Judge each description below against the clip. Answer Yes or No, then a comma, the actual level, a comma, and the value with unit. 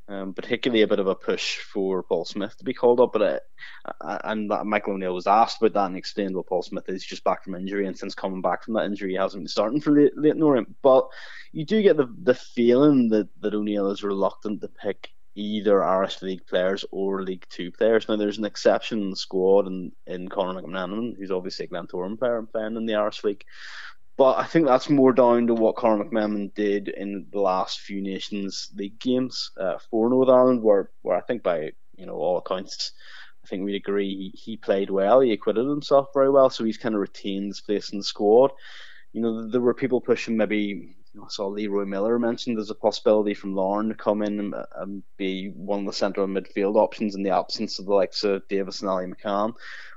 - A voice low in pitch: Yes, low, 105 Hz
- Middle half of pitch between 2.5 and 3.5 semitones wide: Yes, average, 2.9 semitones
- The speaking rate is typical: No, fast, 230 wpm